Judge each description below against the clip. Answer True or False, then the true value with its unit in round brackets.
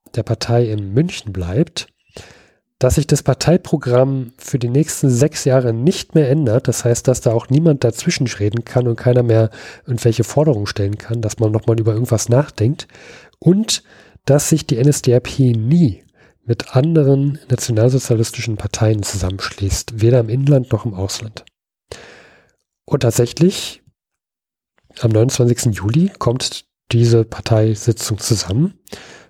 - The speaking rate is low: False (135 wpm)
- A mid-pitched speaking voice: False (120 Hz)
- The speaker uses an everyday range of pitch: True (3.7 semitones)